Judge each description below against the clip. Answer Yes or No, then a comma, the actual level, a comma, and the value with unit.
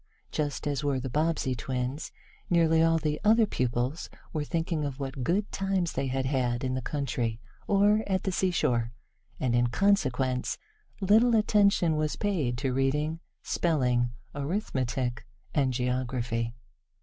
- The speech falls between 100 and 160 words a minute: Yes, average, 140 wpm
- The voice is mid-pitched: Yes, medium, 145 Hz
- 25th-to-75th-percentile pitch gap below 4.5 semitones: No, average, 5.2 semitones